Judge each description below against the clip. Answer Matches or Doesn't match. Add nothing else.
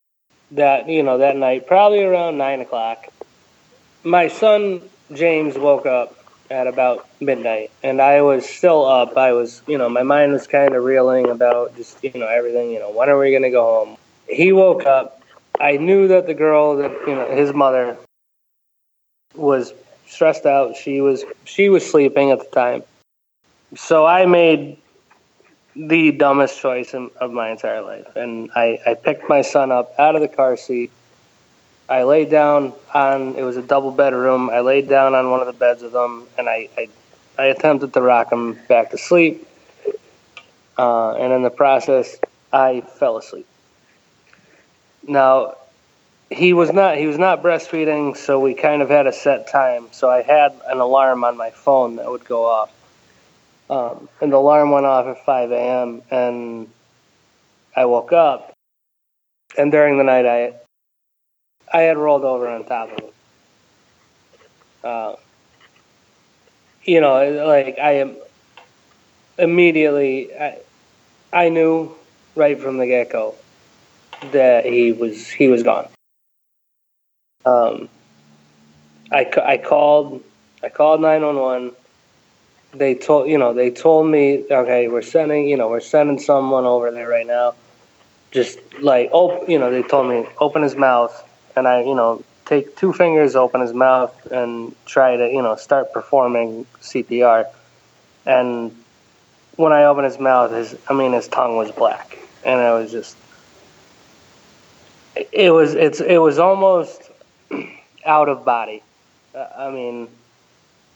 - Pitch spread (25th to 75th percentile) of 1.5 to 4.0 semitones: Matches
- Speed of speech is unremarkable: Matches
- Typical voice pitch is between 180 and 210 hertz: Doesn't match